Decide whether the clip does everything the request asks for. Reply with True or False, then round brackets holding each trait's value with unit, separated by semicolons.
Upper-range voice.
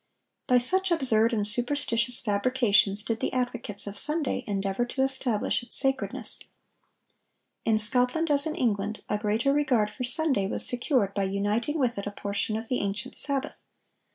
True (240 Hz)